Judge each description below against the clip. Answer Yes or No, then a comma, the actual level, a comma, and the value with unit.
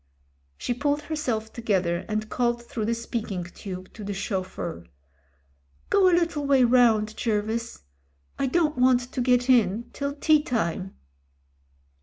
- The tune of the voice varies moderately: Yes, average, 3.9 semitones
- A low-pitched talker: No, high, 235 Hz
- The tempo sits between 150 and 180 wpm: Yes, average, 160 wpm